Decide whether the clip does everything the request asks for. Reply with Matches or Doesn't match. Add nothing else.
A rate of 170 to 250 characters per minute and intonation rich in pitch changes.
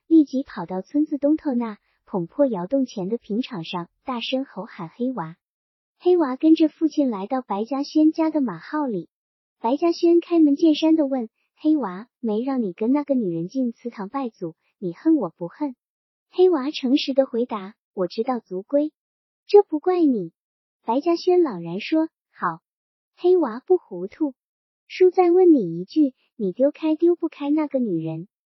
Matches